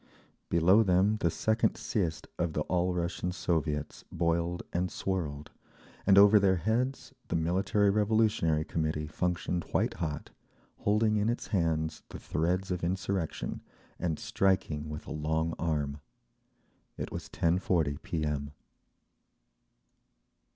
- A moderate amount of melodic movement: Yes, average, 3.6 semitones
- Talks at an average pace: No, slow, 125 wpm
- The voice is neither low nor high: No, very low, 85 Hz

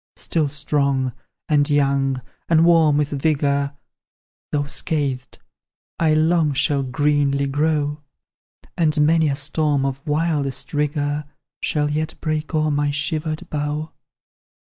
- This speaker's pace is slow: Yes, slow, 120 wpm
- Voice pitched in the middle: Yes, medium, 145 Hz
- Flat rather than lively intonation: Yes, narrow, 1.6 semitones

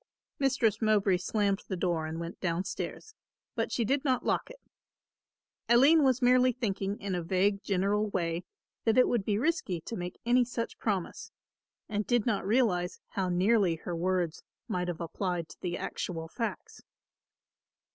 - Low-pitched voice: No, high, 200 Hz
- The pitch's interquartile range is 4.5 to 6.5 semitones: Yes, average, 5.0 semitones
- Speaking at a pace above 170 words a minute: No, average, 165 wpm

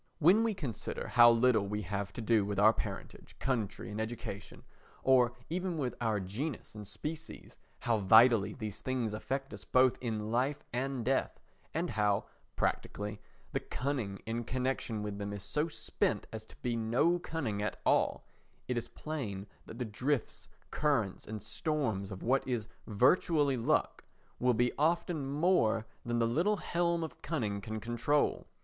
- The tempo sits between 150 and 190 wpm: Yes, average, 165 wpm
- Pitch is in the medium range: No, low, 120 Hz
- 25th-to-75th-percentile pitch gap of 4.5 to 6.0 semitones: Yes, average, 4.9 semitones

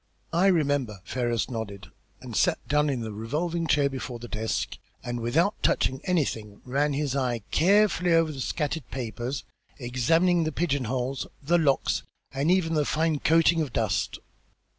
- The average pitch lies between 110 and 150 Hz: Yes, medium, 140 Hz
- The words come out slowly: No, average, 160 wpm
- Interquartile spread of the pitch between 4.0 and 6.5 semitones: Yes, average, 5.2 semitones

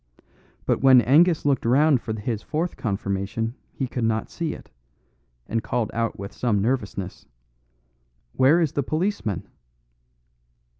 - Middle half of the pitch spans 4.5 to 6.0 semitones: Yes, average, 4.9 semitones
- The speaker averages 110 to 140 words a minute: Yes, slow, 135 wpm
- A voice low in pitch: Yes, low, 120 Hz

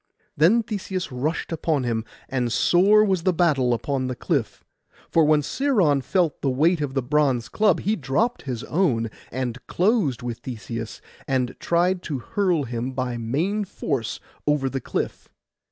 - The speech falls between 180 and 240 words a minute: No, average, 160 wpm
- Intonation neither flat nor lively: No, wide, 6.2 semitones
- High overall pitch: No, medium, 145 Hz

